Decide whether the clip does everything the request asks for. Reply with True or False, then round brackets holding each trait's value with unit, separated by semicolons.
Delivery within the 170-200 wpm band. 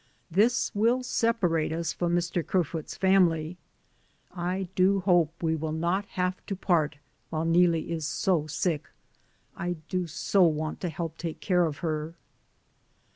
False (150 wpm)